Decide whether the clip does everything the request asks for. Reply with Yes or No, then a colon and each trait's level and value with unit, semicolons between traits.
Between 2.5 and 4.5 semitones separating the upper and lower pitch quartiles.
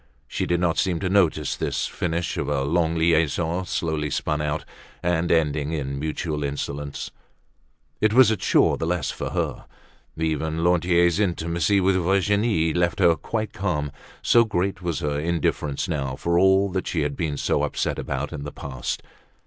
Yes: average, 3.1 semitones